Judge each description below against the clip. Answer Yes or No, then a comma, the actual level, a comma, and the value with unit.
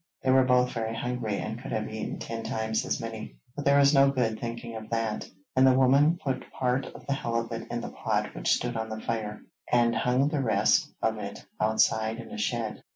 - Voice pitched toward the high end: No, low, 120 Hz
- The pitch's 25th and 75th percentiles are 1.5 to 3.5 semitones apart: Yes, average, 2.8 semitones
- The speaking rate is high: Yes, fast, 220 wpm